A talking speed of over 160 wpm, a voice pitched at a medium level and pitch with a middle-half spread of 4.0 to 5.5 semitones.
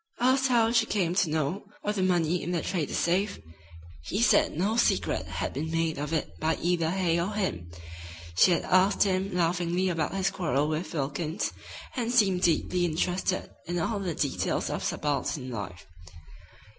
No: average, 170 wpm; medium, 175 Hz; average, 3.4 semitones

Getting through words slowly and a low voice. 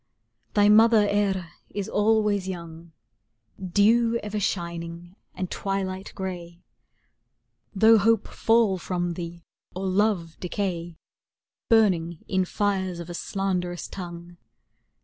No: slow, 110 wpm; high, 190 Hz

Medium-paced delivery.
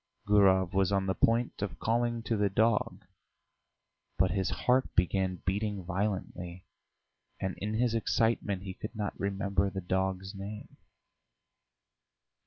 No: slow, 130 wpm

